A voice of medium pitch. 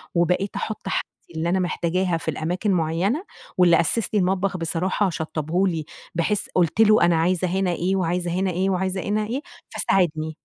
Yes: medium, 180 Hz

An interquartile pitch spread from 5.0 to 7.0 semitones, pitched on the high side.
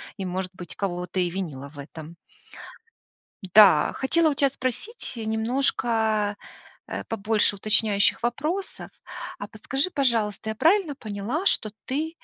Yes: wide, 5.6 semitones; high, 220 Hz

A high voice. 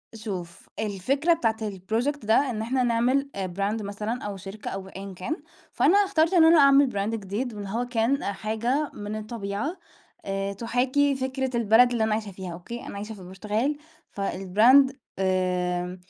Yes: high, 220 Hz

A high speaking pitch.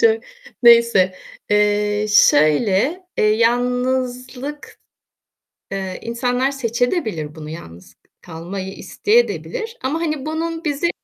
Yes: high, 235 Hz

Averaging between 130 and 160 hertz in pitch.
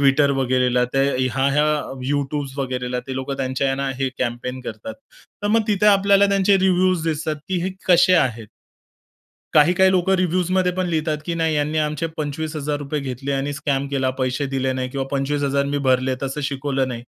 Yes: medium, 140 Hz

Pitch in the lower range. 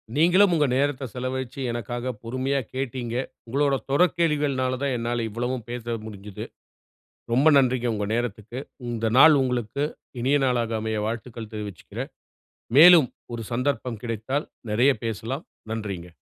Yes: low, 125 Hz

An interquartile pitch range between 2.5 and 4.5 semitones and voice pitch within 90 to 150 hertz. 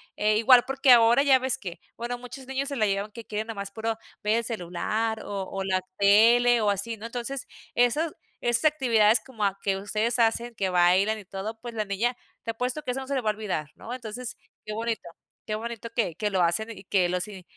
No: average, 3.1 semitones; high, 225 Hz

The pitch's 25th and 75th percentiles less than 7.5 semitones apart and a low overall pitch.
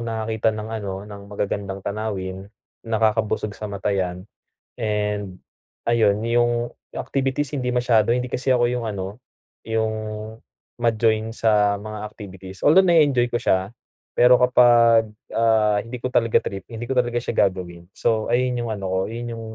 Yes: average, 2.7 semitones; low, 110 Hz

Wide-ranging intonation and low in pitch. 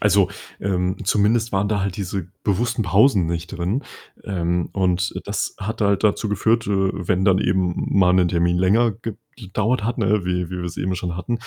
No: average, 2.7 semitones; very low, 95 Hz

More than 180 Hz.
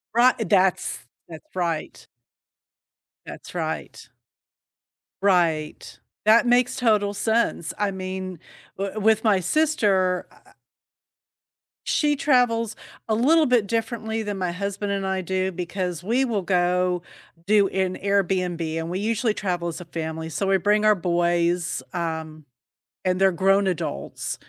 Yes: high, 190 Hz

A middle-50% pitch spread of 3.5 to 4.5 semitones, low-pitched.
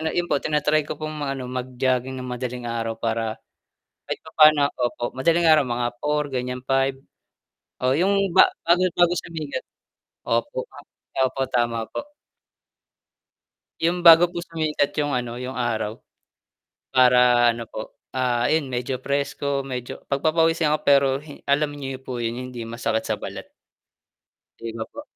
Yes: average, 3.9 semitones; low, 130 Hz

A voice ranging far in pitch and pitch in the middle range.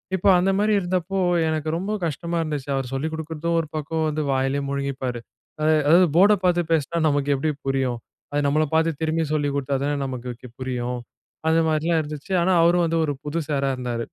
No: average, 3.3 semitones; medium, 155 Hz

